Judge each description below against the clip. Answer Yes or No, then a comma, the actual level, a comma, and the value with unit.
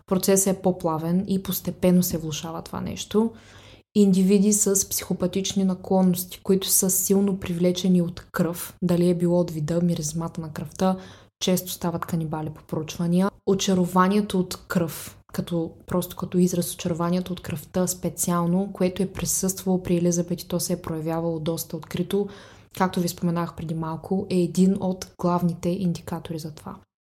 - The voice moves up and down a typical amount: No, narrow, 1.9 semitones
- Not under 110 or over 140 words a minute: No, average, 150 wpm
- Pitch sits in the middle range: Yes, medium, 180 Hz